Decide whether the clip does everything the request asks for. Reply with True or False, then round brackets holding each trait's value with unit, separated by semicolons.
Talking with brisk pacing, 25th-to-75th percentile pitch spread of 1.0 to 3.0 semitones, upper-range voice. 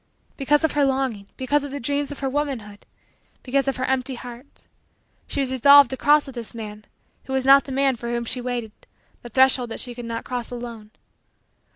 True (210 wpm; 2.7 semitones; 260 Hz)